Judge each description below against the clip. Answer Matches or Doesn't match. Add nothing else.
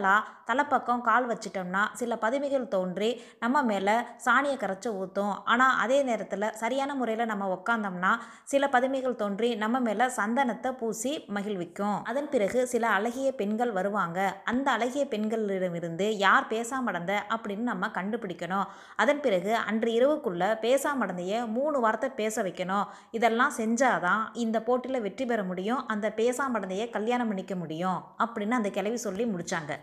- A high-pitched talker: Matches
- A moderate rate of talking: Doesn't match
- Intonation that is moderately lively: Matches